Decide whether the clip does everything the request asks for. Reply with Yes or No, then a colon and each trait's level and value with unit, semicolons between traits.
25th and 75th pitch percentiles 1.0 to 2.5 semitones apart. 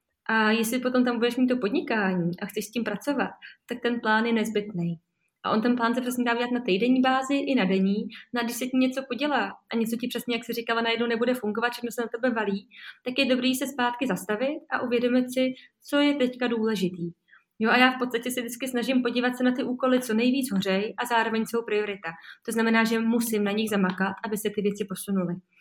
No: average, 2.9 semitones